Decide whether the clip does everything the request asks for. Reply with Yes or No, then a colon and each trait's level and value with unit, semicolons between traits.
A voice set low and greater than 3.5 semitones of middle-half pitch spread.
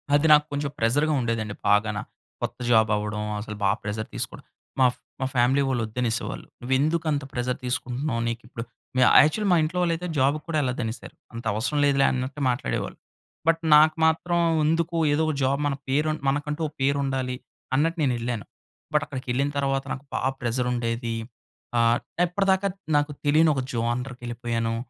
Yes: low, 130 Hz; average, 4.1 semitones